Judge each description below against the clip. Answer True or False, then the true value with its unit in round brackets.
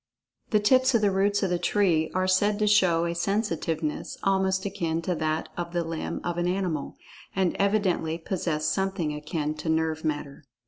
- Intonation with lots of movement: False (3.5 semitones)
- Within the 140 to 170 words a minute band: False (180 wpm)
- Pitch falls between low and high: True (175 Hz)